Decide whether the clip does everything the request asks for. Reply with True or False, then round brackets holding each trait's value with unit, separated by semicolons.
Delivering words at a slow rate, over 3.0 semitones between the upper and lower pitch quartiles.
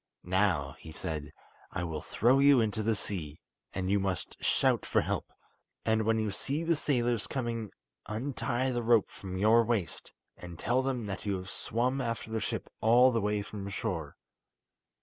False (175 wpm; 4.0 semitones)